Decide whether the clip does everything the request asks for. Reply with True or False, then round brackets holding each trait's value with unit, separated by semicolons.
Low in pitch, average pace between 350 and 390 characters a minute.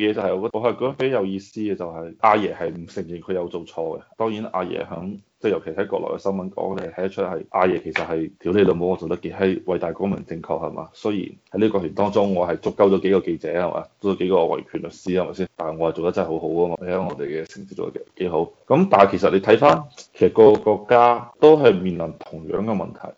True (95 Hz; 375 characters per minute)